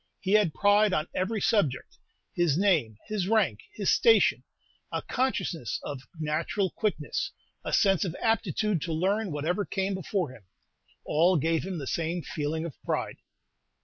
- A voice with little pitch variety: No, average, 4.6 semitones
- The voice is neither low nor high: Yes, medium, 180 Hz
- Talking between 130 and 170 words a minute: Yes, average, 150 wpm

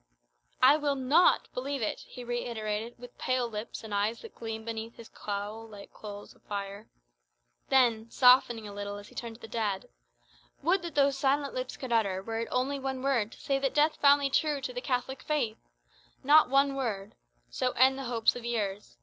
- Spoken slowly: No, average, 200 wpm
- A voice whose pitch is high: Yes, high, 240 Hz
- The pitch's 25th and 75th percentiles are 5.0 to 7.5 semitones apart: No, average, 3.9 semitones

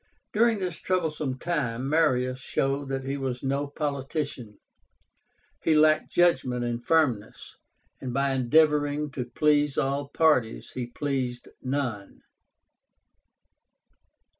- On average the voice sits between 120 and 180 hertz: Yes, medium, 140 Hz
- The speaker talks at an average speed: No, slow, 110 wpm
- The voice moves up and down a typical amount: Yes, average, 3.1 semitones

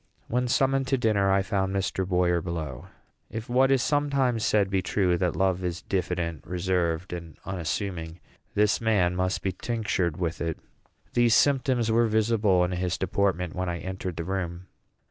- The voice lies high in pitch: No, very low, 95 Hz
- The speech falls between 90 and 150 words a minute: No, average, 165 wpm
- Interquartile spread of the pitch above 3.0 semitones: Yes, average, 4.0 semitones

